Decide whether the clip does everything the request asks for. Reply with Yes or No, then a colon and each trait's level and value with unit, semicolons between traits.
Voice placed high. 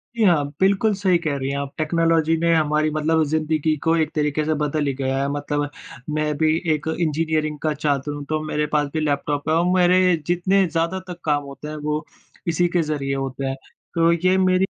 No: medium, 155 Hz